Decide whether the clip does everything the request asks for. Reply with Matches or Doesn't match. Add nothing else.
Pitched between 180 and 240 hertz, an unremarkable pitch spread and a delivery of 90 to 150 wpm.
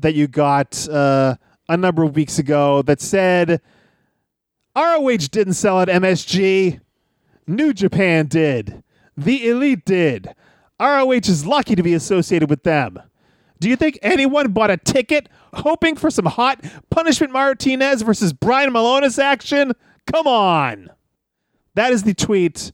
Doesn't match